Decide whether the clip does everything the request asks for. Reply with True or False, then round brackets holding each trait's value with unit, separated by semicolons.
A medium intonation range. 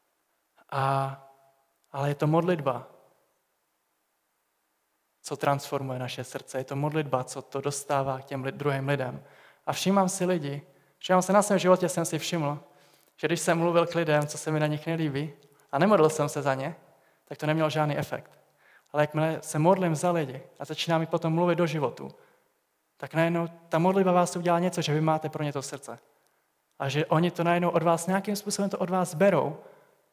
True (3.5 semitones)